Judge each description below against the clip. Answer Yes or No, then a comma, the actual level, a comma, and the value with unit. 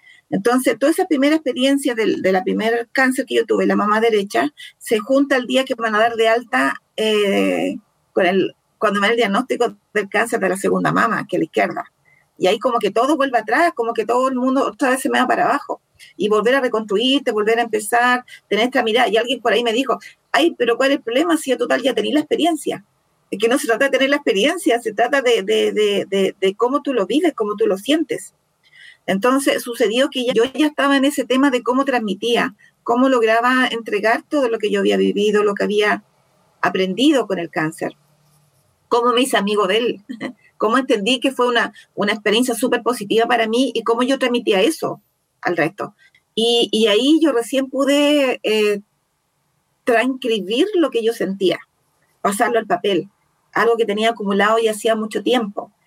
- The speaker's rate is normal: No, fast, 205 wpm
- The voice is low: No, high, 240 Hz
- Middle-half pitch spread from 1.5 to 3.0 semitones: No, average, 3.7 semitones